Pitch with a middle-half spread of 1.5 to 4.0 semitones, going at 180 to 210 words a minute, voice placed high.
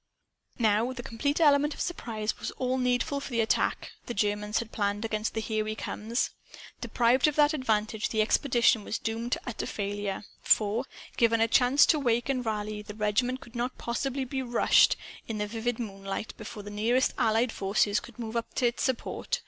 Yes: average, 3.0 semitones; average, 190 wpm; high, 230 Hz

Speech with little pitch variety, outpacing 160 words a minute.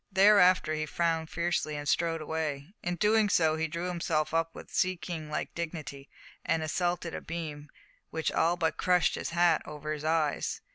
Yes: narrow, 2.1 semitones; average, 180 wpm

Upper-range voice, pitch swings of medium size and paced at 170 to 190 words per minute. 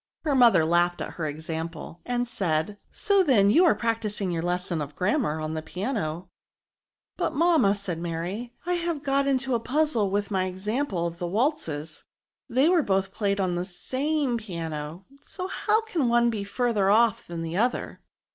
No: high, 205 Hz; wide, 7.0 semitones; average, 185 wpm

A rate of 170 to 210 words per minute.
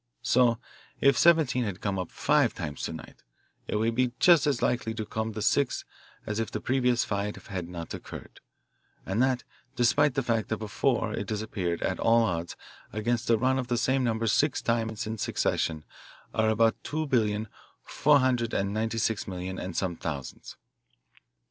Yes: average, 180 wpm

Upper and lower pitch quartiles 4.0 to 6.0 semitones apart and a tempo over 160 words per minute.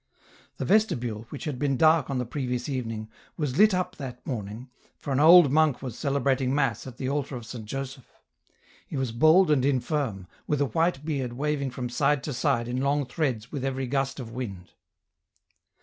No: average, 3.1 semitones; average, 190 wpm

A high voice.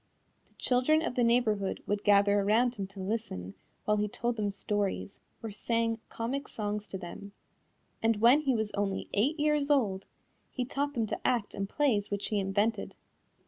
Yes: high, 215 Hz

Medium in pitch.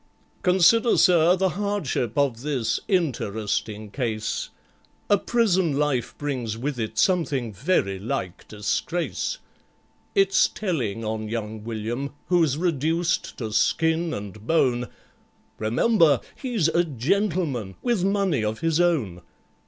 Yes: medium, 145 Hz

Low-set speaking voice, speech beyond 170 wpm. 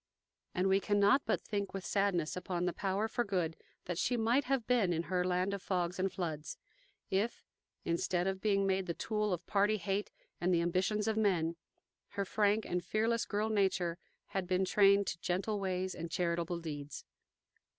No: high, 190 Hz; average, 180 wpm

